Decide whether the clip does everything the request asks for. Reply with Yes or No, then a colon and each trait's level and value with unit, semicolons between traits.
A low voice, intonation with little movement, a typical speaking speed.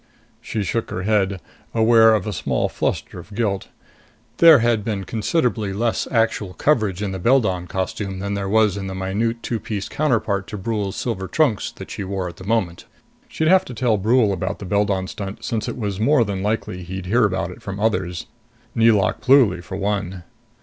No: low, 105 Hz; average, 3.1 semitones; average, 190 wpm